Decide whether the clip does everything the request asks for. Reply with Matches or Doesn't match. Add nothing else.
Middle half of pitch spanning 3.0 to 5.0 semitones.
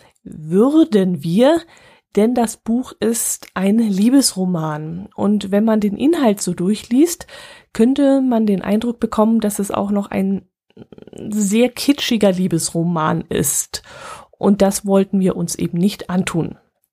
Matches